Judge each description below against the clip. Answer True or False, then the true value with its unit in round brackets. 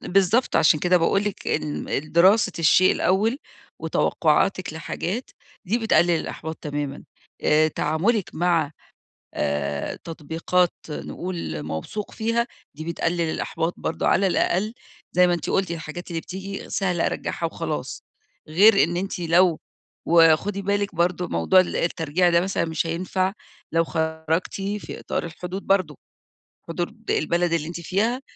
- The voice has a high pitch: False (175 Hz)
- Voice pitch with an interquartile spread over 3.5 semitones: False (3.2 semitones)